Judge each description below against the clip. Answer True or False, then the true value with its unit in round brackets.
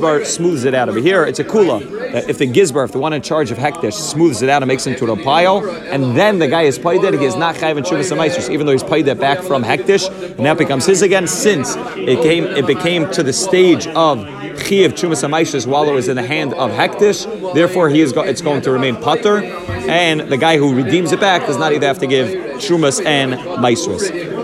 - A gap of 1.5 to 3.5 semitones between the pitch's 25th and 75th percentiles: False (4.2 semitones)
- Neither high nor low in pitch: True (155 Hz)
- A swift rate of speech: True (250 wpm)